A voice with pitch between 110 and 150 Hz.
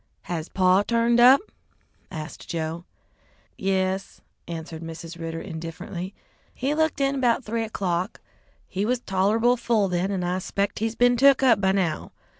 No: high, 195 Hz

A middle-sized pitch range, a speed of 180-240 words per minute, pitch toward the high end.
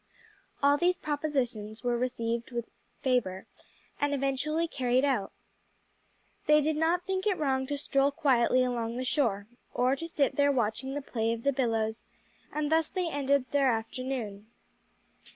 No: average, 3.6 semitones; average, 150 wpm; very high, 265 Hz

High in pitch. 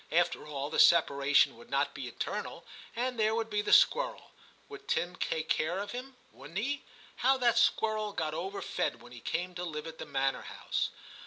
No: medium, 180 Hz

